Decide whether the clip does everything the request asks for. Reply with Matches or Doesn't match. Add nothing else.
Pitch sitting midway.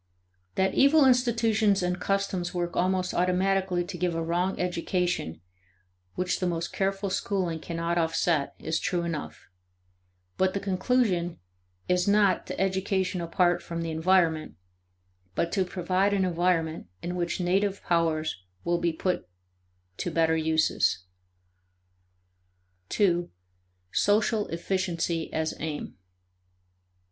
Matches